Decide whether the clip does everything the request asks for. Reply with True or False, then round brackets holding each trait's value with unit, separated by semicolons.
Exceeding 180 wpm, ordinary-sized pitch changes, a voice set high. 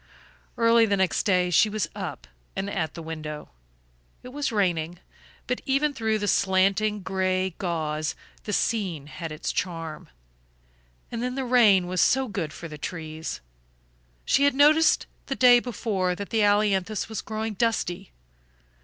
False (155 wpm; 4.6 semitones; 200 Hz)